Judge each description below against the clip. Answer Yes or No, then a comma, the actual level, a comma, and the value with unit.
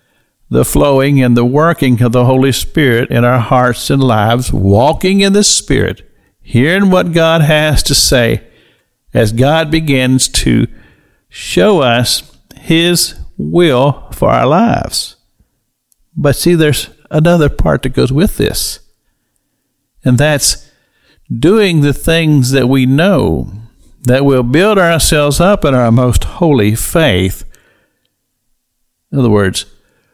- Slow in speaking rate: Yes, slow, 130 wpm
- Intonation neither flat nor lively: Yes, average, 4.6 semitones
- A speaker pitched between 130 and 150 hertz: Yes, low, 135 Hz